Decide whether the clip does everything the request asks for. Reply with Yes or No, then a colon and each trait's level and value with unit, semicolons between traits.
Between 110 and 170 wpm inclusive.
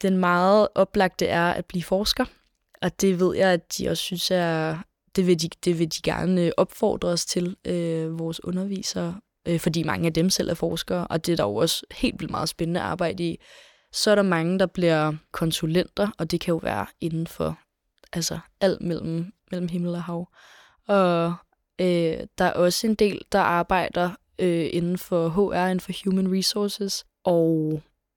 No: average, 185 wpm